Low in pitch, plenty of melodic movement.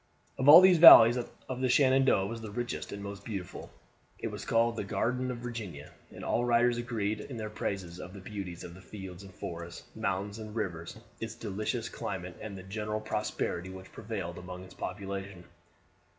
No: low, 105 Hz; average, 3.9 semitones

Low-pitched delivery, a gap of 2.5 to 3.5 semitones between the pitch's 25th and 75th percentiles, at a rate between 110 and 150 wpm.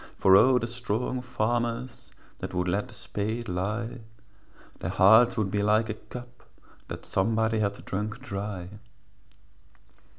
Yes: low, 110 Hz; average, 2.9 semitones; average, 140 wpm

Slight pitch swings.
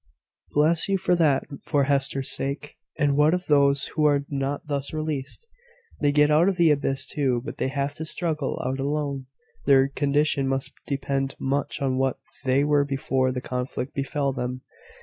Yes: narrow, 1.7 semitones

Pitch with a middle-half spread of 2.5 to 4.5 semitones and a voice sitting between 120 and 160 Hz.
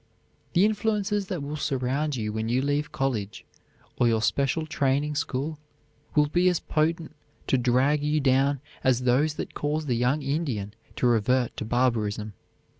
Yes: average, 3.8 semitones; medium, 140 Hz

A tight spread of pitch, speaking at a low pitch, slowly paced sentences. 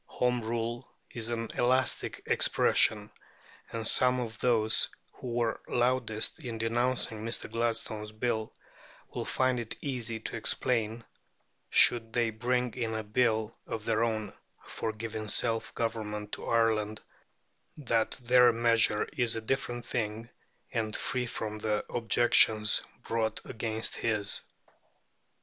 Yes: narrow, 1.6 semitones; low, 115 Hz; slow, 125 wpm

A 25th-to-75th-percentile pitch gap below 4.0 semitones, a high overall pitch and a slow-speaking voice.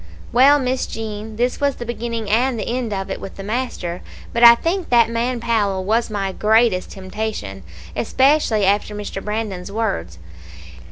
No: average, 3.2 semitones; high, 220 Hz; average, 165 wpm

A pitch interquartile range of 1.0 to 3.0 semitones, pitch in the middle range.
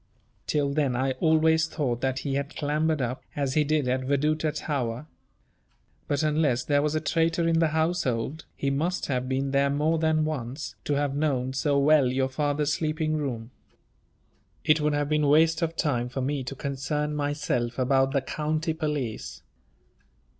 Yes: narrow, 2.6 semitones; medium, 145 Hz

